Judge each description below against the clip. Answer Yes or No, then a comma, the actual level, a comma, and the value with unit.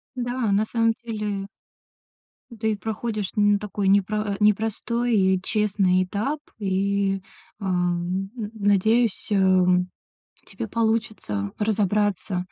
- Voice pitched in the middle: No, high, 205 Hz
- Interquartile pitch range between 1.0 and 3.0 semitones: Yes, narrow, 2.4 semitones